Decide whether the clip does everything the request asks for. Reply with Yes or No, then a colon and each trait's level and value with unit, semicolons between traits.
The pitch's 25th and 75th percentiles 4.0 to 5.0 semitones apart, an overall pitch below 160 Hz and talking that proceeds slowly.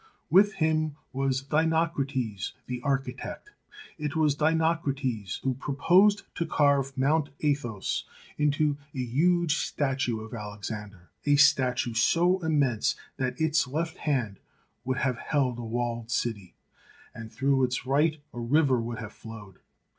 Yes: average, 4.3 semitones; low, 135 Hz; slow, 130 wpm